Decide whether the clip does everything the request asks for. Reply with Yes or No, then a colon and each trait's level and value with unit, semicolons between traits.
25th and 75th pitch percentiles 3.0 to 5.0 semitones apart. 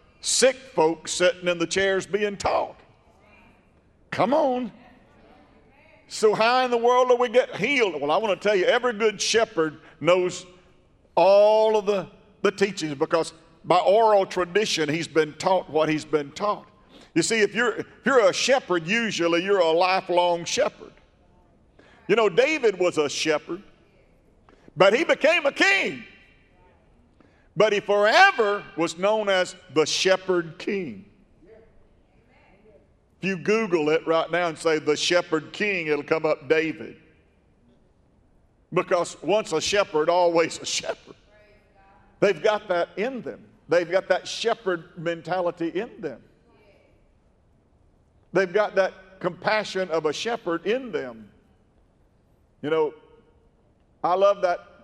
Yes: average, 4.3 semitones